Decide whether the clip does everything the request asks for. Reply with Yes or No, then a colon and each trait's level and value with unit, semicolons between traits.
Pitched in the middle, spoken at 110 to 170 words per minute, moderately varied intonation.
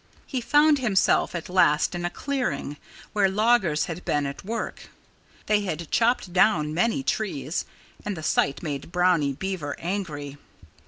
No: medium, 180 Hz; average, 150 wpm; wide, 6.1 semitones